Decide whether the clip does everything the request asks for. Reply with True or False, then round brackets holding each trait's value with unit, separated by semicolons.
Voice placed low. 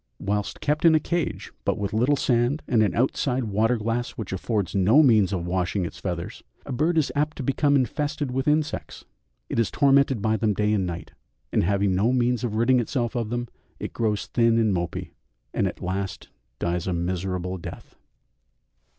True (115 Hz)